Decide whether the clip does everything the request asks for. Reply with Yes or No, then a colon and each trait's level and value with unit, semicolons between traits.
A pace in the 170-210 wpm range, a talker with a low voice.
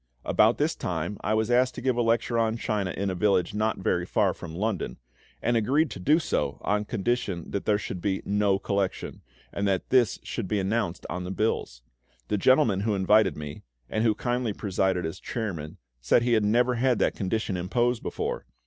Yes: average, 200 wpm; low, 105 Hz